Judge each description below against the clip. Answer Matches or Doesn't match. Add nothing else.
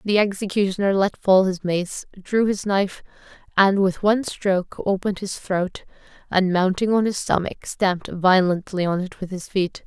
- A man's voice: Doesn't match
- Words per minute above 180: Doesn't match